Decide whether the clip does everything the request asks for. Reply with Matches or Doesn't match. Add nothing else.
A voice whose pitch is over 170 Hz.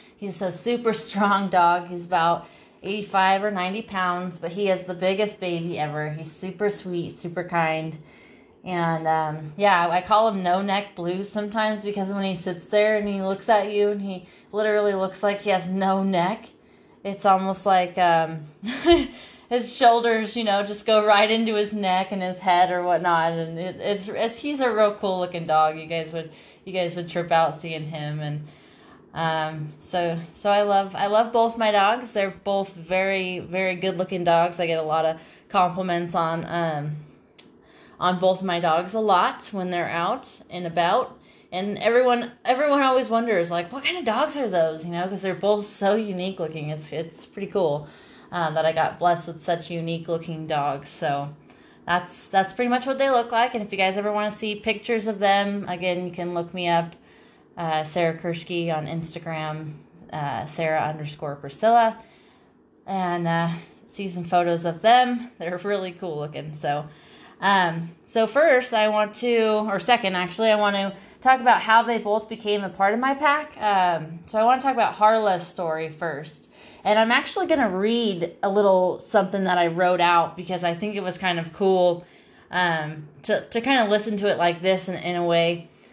Matches